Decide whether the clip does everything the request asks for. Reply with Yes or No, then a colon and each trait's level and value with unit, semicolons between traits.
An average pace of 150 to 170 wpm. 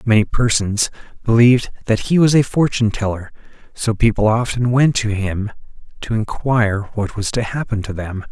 Yes: average, 165 wpm